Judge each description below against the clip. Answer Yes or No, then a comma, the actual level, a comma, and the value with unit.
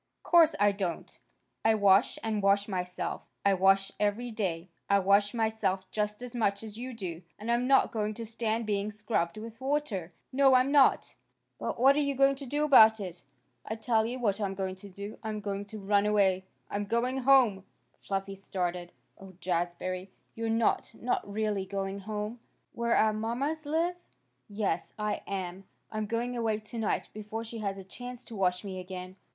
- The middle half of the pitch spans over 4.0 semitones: No, average, 3.1 semitones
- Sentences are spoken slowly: No, average, 180 wpm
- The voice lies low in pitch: No, high, 210 Hz